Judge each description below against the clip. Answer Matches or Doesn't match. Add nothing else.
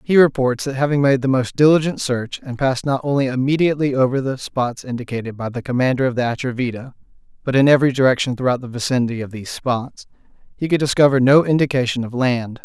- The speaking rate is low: Doesn't match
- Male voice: Matches